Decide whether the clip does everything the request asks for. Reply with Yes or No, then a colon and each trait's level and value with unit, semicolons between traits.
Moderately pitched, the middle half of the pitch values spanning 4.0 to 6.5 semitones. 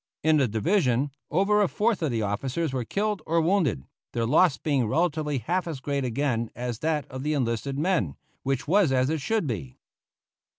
Yes: medium, 145 Hz; average, 5.2 semitones